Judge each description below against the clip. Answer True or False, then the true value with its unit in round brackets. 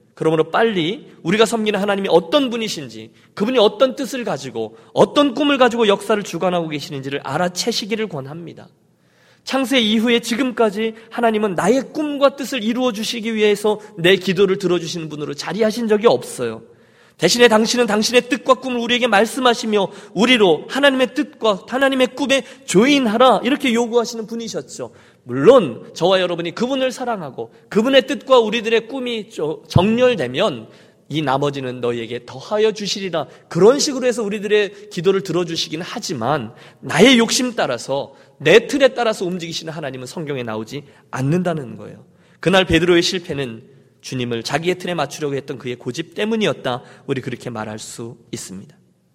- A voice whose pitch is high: True (210 Hz)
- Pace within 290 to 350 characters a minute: False (380 characters per minute)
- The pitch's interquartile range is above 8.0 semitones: False (7.0 semitones)